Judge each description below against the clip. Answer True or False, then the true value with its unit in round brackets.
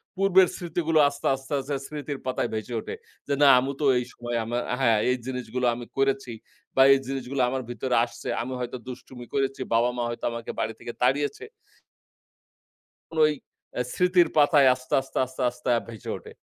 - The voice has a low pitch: True (130 Hz)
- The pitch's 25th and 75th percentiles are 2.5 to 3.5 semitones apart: True (2.9 semitones)